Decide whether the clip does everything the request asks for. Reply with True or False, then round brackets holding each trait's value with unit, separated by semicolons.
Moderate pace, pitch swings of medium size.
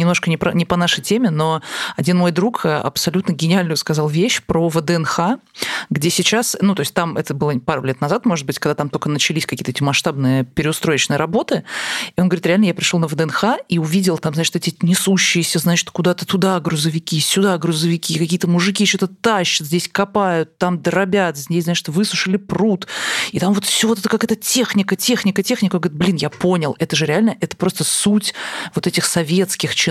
False (195 wpm; 3.3 semitones)